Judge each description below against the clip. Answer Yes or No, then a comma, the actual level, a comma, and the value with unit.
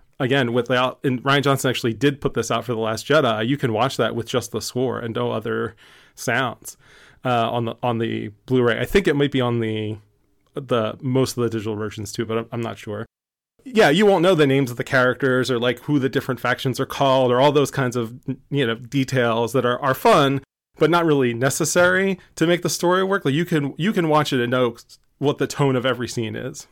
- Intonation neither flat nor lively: Yes, average, 3.1 semitones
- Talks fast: Yes, fast, 235 wpm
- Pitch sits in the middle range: No, low, 130 Hz